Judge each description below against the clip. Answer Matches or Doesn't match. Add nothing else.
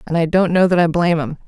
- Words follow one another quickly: Matches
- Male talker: Doesn't match